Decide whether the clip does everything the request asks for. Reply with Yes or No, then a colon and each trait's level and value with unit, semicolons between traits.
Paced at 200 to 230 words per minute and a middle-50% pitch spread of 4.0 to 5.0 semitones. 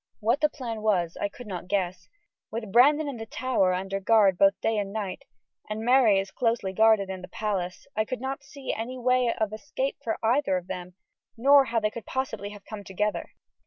Yes: fast, 205 wpm; average, 4.3 semitones